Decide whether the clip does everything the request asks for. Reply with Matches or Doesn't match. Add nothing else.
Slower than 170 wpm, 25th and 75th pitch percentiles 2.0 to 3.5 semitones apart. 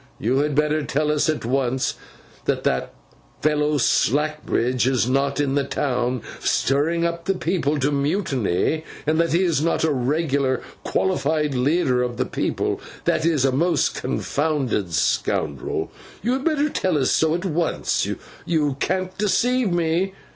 Doesn't match